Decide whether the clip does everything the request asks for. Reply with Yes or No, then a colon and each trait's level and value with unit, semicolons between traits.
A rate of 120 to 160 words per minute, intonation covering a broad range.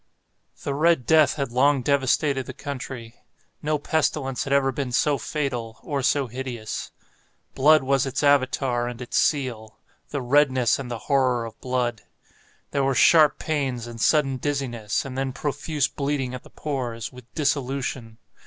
No: average, 155 wpm; narrow, 2.6 semitones